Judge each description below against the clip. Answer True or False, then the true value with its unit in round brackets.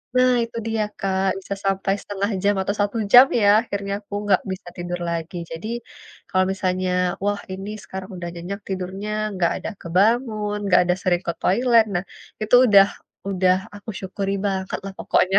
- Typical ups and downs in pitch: False (1.8 semitones)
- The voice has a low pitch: False (195 Hz)